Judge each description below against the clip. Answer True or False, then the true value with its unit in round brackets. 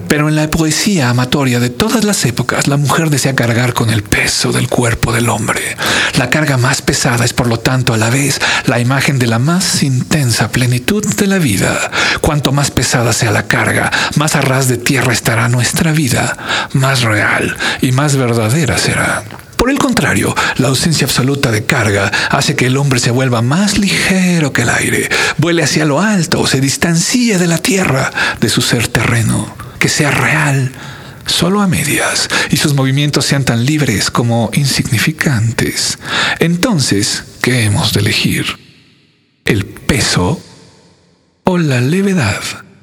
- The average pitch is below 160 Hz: True (135 Hz)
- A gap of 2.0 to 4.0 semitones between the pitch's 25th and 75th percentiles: False (4.4 semitones)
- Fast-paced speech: False (165 wpm)